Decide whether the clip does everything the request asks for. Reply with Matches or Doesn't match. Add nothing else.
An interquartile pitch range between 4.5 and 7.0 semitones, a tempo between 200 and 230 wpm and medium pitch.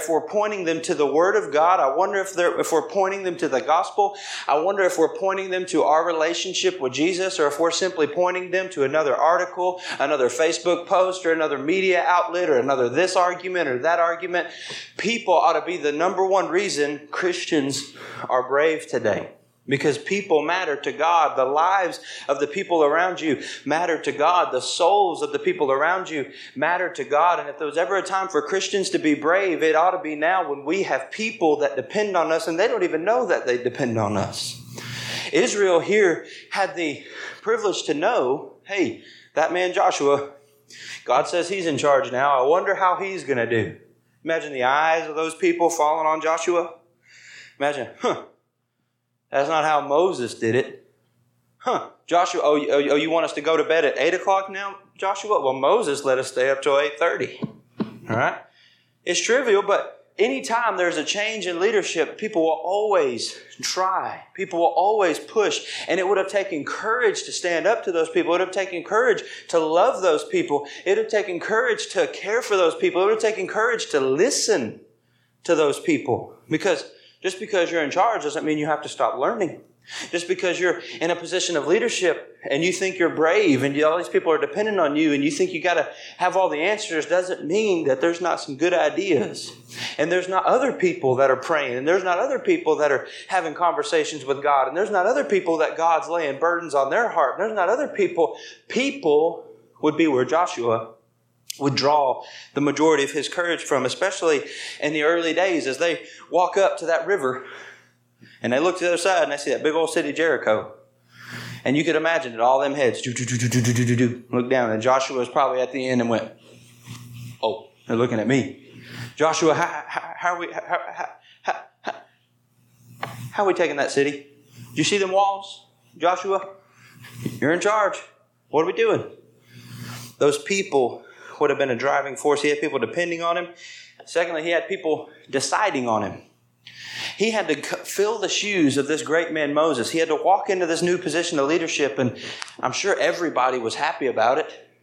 Matches